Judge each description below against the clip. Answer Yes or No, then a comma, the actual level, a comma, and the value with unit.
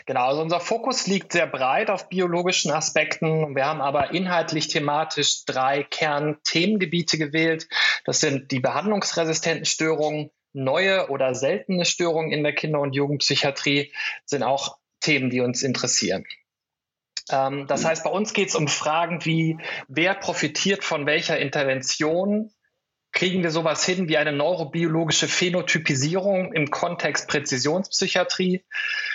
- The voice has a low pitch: No, medium, 160 Hz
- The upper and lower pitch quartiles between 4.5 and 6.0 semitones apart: No, average, 3.6 semitones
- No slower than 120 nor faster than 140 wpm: Yes, average, 130 wpm